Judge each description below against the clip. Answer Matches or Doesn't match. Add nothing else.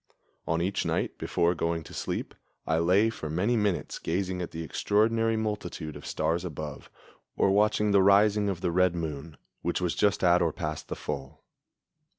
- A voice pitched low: Matches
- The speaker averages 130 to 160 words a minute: Doesn't match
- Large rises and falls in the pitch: Doesn't match